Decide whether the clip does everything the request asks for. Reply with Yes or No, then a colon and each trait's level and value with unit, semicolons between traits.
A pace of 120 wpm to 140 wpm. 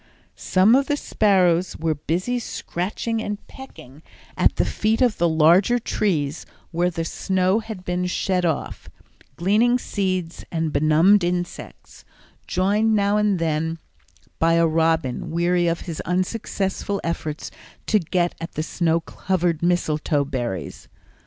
Yes: slow, 135 wpm